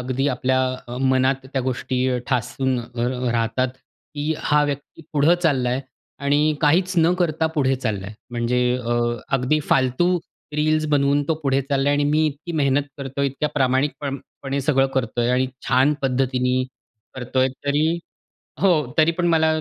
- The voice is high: No, low, 135 Hz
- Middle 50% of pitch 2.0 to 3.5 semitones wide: Yes, average, 2.7 semitones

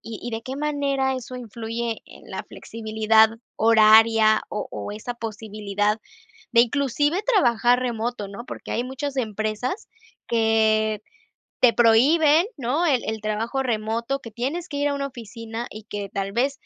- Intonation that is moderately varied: Yes, average, 3.4 semitones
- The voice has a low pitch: No, high, 230 Hz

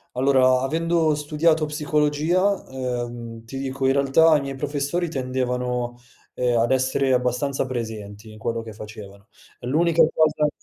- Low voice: Yes, low, 130 Hz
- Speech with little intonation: No, average, 3.7 semitones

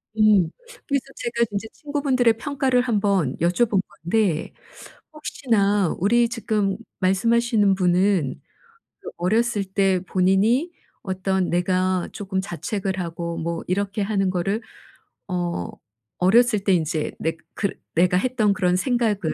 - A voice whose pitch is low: No, high, 195 Hz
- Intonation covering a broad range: No, average, 3.9 semitones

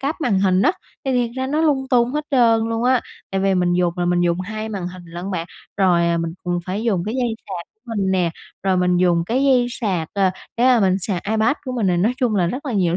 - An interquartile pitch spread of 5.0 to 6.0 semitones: Yes, average, 5.3 semitones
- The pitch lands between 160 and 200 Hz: Yes, high, 195 Hz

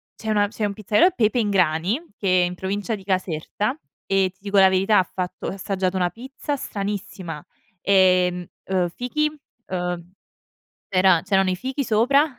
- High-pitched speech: Yes, high, 195 Hz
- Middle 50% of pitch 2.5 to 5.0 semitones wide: Yes, average, 2.8 semitones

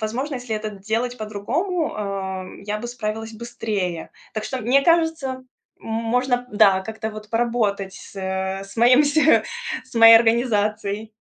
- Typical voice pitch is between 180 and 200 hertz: No, high, 220 Hz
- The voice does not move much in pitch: No, average, 3.2 semitones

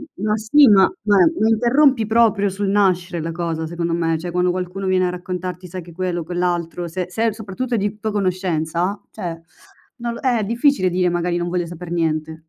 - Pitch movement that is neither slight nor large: Yes, average, 3.3 semitones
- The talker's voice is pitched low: No, medium, 180 Hz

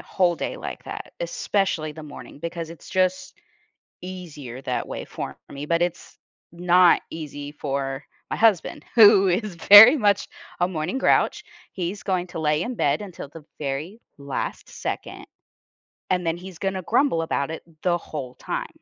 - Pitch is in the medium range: Yes, medium, 175 Hz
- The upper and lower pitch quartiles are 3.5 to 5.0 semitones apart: Yes, average, 4.0 semitones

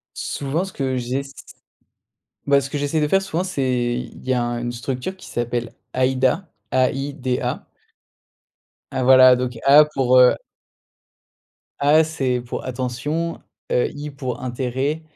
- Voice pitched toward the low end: Yes, low, 130 Hz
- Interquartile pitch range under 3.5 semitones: Yes, average, 2.8 semitones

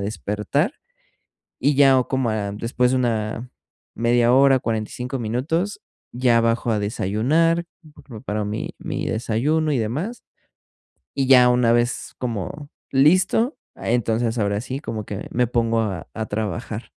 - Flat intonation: No, average, 3.5 semitones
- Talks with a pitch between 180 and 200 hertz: No, low, 120 Hz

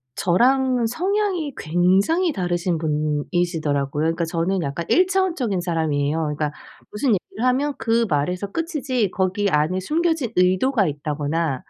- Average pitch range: No, wide, 8.5 semitones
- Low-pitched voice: No, medium, 185 Hz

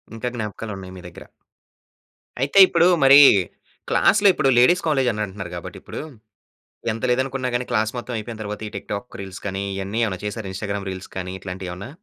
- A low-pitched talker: Yes, low, 105 Hz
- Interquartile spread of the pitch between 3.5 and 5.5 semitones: Yes, average, 4.5 semitones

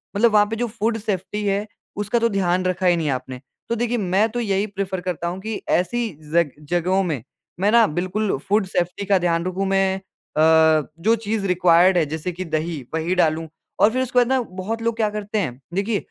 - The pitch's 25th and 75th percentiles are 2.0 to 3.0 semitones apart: No, average, 3.6 semitones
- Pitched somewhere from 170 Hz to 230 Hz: Yes, high, 190 Hz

